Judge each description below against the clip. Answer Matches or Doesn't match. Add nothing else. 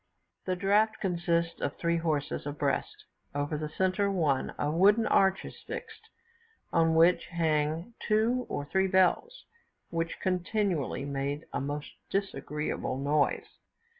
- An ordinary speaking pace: Doesn't match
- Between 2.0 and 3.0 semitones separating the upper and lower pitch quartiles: Doesn't match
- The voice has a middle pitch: Matches